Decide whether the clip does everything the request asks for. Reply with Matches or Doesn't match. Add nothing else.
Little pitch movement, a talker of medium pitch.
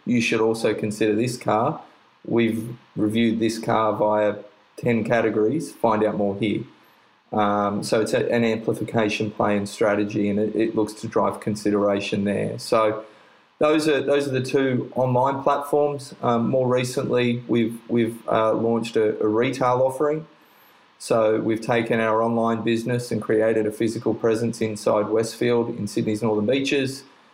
Doesn't match